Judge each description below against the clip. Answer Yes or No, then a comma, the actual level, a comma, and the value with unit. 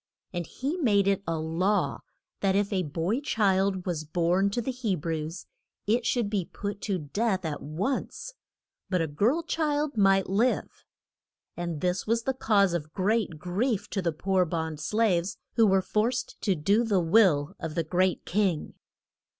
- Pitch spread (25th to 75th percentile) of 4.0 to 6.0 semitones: Yes, average, 4.6 semitones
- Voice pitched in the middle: No, high, 195 Hz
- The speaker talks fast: No, average, 170 wpm